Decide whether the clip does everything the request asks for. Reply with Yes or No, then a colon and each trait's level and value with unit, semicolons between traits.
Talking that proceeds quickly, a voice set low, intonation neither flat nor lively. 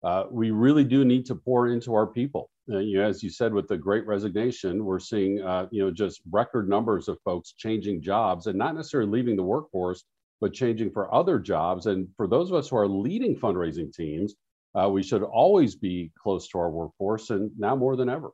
Yes: fast, 220 wpm; low, 105 Hz; average, 3.7 semitones